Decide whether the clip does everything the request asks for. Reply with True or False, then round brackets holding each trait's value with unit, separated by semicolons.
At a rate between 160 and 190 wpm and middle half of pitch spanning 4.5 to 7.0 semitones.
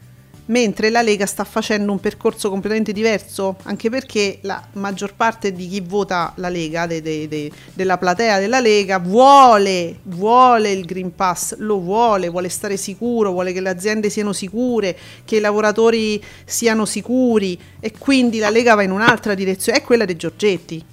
False (170 wpm; 3.1 semitones)